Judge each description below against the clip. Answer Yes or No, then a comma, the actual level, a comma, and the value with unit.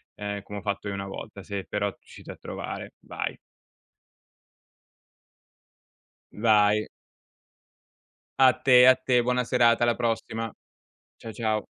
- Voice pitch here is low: Yes, low, 110 Hz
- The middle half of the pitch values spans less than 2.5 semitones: No, average, 2.8 semitones